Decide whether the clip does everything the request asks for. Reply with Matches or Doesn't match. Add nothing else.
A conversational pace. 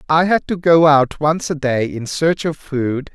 Doesn't match